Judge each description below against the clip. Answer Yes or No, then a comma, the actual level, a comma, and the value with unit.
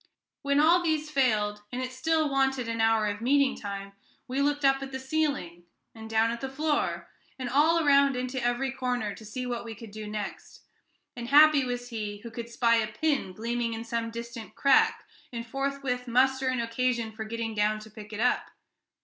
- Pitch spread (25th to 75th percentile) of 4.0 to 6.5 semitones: No, average, 3.5 semitones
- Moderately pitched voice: No, high, 245 Hz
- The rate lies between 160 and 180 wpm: No, average, 200 wpm